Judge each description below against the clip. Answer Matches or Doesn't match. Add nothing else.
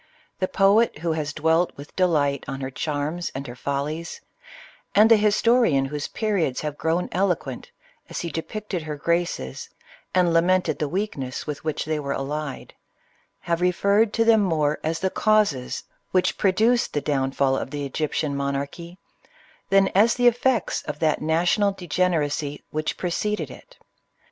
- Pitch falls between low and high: Matches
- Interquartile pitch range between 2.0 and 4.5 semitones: Doesn't match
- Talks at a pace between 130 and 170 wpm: Matches